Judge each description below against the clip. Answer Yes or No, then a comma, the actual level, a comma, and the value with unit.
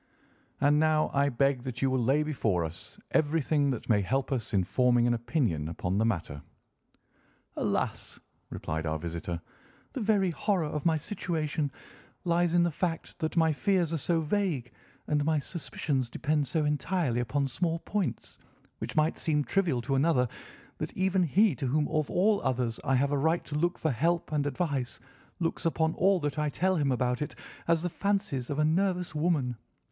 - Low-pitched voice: No, medium, 150 Hz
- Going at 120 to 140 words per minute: No, average, 185 wpm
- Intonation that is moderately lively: Yes, average, 4.8 semitones